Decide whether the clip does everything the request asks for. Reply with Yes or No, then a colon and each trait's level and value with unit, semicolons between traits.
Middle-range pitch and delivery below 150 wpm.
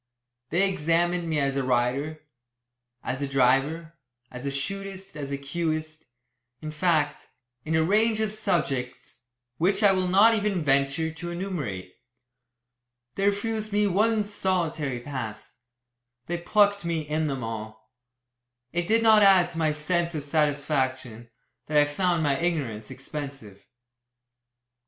Yes: medium, 155 Hz; slow, 135 wpm